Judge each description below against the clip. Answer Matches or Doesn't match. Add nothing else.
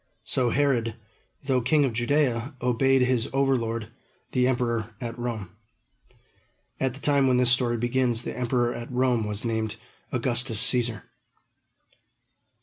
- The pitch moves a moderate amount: Doesn't match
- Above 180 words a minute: Doesn't match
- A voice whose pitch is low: Matches